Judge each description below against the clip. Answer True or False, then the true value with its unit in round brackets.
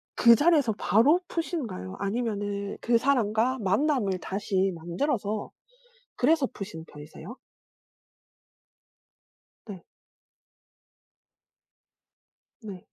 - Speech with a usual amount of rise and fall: True (5.0 semitones)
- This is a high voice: True (215 Hz)